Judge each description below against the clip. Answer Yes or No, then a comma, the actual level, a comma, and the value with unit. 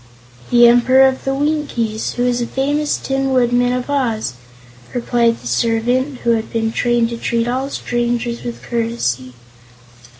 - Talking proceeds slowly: No, average, 155 wpm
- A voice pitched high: Yes, high, 240 Hz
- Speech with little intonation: Yes, narrow, 2.1 semitones